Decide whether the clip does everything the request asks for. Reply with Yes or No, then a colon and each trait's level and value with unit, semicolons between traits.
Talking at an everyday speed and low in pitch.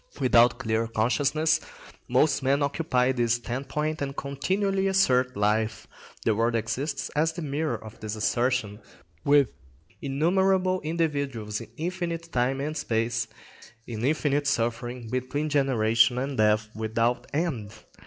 No: slow, 125 wpm; low, 130 Hz